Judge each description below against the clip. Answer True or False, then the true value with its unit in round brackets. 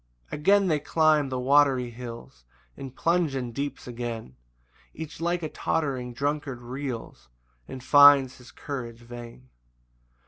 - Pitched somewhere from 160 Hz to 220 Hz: False (135 Hz)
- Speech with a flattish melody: False (3.4 semitones)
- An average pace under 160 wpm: True (135 wpm)